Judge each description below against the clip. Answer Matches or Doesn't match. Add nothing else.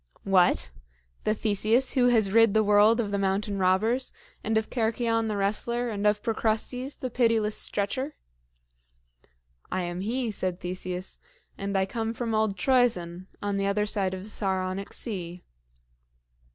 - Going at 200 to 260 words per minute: Doesn't match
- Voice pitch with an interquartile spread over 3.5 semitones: Doesn't match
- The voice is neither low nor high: Doesn't match